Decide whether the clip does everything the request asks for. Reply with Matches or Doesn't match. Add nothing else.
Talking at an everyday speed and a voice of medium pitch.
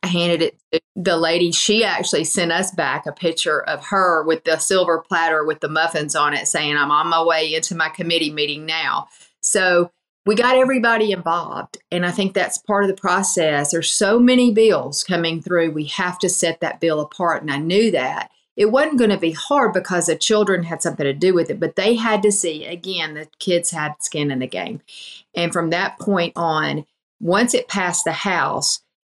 Doesn't match